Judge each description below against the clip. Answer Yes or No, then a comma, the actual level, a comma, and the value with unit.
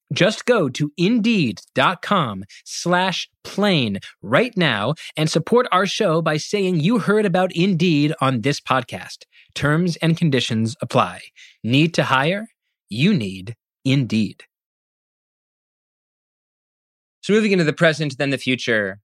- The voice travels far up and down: Yes, wide, 6.2 semitones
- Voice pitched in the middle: Yes, medium, 160 Hz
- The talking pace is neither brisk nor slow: No, slow, 125 wpm